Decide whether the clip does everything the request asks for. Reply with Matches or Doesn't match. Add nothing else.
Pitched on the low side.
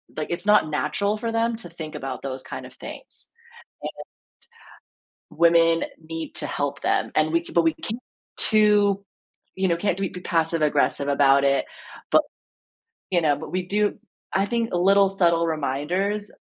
Doesn't match